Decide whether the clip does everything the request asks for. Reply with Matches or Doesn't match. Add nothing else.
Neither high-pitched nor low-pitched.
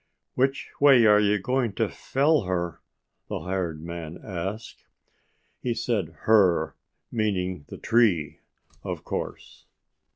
Doesn't match